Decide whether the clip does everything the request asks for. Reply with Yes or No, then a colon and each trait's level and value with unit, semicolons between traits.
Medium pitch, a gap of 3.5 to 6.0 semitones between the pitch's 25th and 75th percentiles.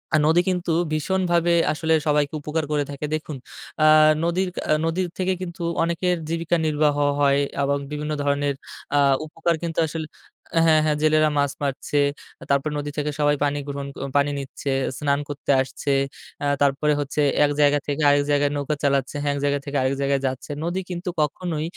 No: medium, 150 Hz; narrow, 2.4 semitones